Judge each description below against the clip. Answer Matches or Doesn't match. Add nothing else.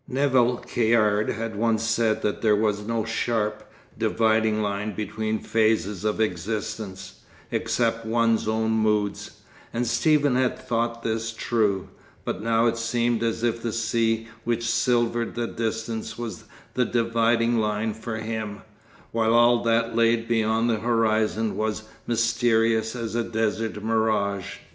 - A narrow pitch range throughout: Matches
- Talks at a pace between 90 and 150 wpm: Matches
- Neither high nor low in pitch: Doesn't match